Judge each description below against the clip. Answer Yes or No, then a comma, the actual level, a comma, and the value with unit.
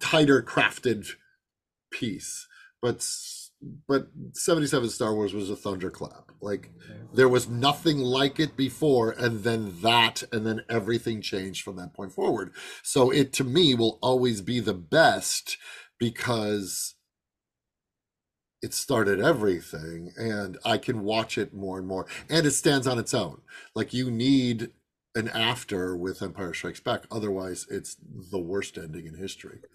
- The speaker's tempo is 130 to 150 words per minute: Yes, average, 145 wpm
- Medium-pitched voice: No, low, 115 Hz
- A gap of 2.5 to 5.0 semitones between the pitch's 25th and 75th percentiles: Yes, average, 4.7 semitones